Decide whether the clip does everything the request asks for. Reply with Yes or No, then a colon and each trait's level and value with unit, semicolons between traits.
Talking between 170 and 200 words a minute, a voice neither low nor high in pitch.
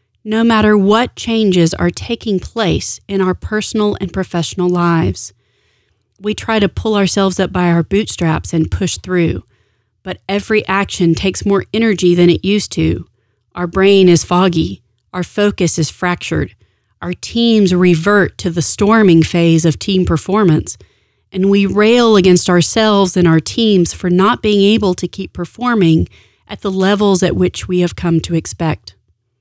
No: average, 160 wpm; medium, 180 Hz